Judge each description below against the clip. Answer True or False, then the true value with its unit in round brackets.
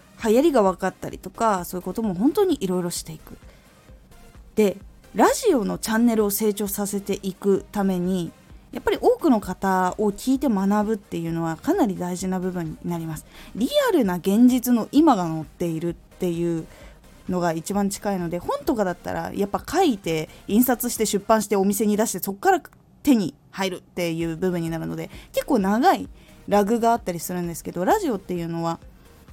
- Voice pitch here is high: True (195 Hz)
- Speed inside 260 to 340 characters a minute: False (370 characters per minute)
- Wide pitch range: False (4.6 semitones)